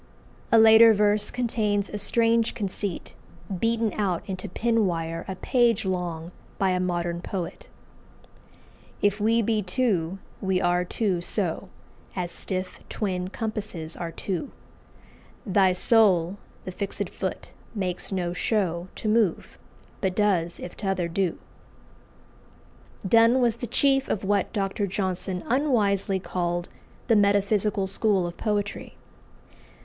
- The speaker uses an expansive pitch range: No, average, 3.2 semitones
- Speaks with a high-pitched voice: Yes, high, 195 Hz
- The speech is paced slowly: Yes, slow, 130 wpm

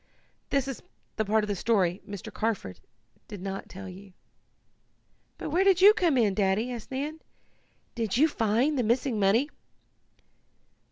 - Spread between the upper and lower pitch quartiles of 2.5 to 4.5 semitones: No, wide, 5.6 semitones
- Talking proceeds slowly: No, average, 155 wpm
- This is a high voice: Yes, high, 225 Hz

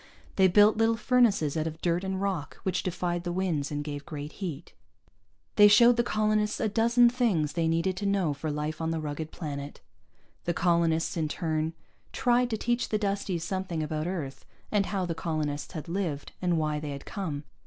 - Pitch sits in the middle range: Yes, medium, 175 Hz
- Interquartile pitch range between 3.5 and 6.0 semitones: Yes, average, 4.6 semitones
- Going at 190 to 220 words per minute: Yes, average, 195 wpm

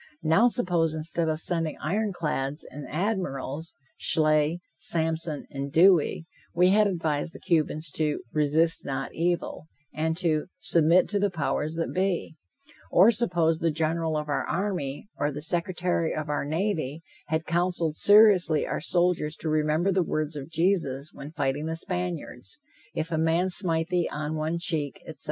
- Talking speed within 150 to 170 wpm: Yes, average, 160 wpm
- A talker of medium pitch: Yes, medium, 160 Hz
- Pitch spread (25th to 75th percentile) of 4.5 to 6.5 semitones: No, narrow, 2.5 semitones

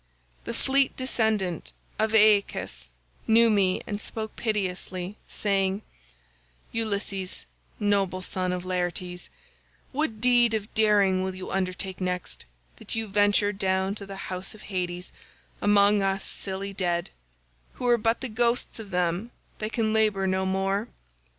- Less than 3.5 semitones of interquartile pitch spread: Yes, average, 2.7 semitones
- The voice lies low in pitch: No, high, 200 Hz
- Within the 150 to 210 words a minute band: No, slow, 135 wpm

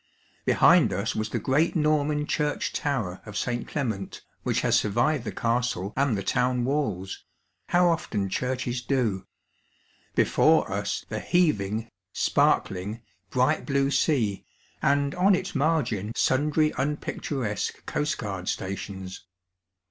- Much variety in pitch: Yes, wide, 6.2 semitones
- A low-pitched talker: Yes, low, 125 Hz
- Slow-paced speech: Yes, slow, 125 wpm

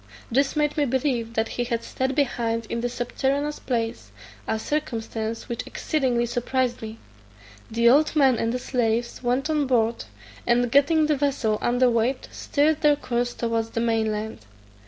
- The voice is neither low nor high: No, high, 245 Hz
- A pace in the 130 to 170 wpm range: Yes, average, 165 wpm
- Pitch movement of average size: Yes, average, 3.3 semitones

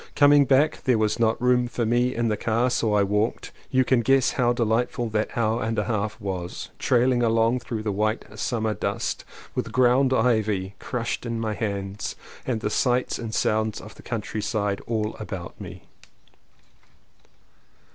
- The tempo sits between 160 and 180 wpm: Yes, average, 165 wpm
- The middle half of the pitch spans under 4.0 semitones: Yes, narrow, 2.4 semitones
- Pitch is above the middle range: No, low, 115 Hz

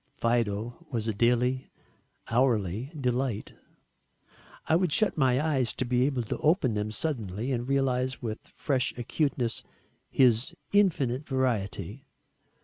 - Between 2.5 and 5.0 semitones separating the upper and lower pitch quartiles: Yes, average, 3.0 semitones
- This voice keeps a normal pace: No, slow, 125 wpm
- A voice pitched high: No, low, 125 Hz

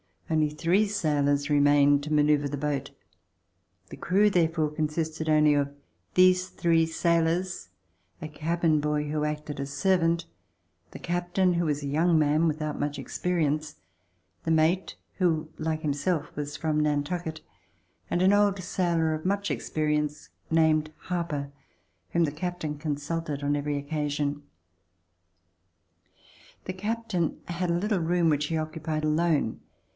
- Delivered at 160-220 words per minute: No, average, 140 wpm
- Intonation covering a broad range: No, narrow, 2.6 semitones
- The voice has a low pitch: No, medium, 155 Hz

